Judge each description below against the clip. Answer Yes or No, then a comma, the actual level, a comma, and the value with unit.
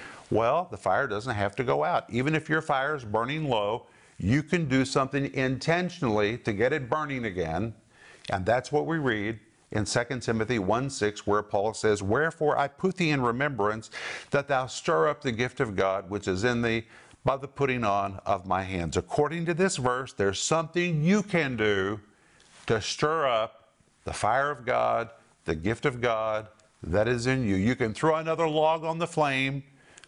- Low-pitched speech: Yes, low, 125 Hz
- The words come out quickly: No, average, 190 wpm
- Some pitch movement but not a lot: No, wide, 5.7 semitones